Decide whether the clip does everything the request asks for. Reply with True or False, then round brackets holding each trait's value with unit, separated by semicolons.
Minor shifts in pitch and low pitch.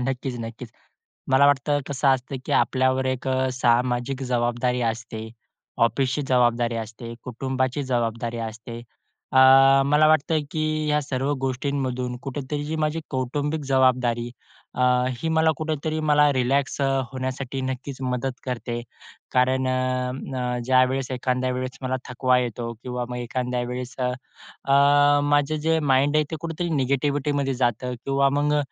True (2.2 semitones; 130 Hz)